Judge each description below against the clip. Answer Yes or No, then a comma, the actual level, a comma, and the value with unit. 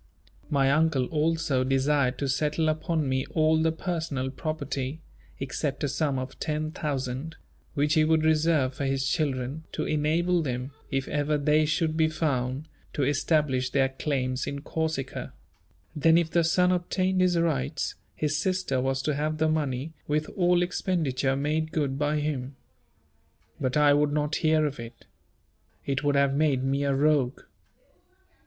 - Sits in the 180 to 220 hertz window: No, medium, 150 Hz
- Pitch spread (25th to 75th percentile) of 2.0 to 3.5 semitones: Yes, average, 2.8 semitones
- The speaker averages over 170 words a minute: No, average, 155 wpm